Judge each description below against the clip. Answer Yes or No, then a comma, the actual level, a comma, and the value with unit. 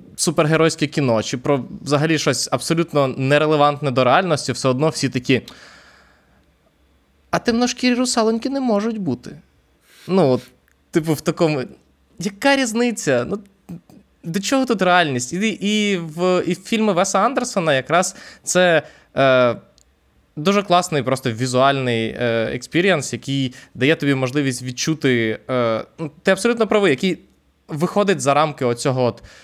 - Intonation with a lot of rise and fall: Yes, wide, 6.9 semitones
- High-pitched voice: No, medium, 155 Hz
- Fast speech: No, average, 135 wpm